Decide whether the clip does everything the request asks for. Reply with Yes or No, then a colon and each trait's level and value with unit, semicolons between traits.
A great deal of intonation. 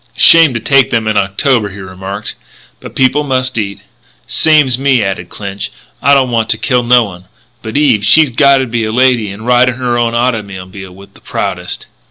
No: average, 4.2 semitones